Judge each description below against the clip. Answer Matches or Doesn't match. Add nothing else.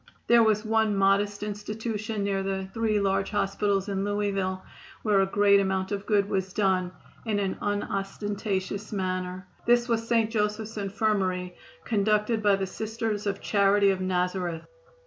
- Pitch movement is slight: Matches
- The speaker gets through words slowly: Doesn't match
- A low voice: Doesn't match